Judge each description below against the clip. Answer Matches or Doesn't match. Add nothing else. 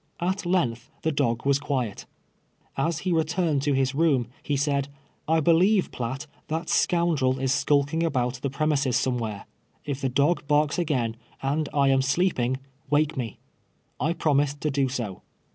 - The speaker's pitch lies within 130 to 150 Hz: Matches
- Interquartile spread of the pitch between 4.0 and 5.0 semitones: Doesn't match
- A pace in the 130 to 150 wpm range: Doesn't match